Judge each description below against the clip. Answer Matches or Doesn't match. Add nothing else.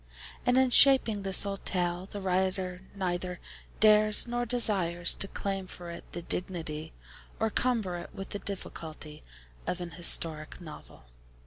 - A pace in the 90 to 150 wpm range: Matches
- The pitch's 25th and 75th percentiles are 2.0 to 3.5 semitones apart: Matches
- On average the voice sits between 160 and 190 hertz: Matches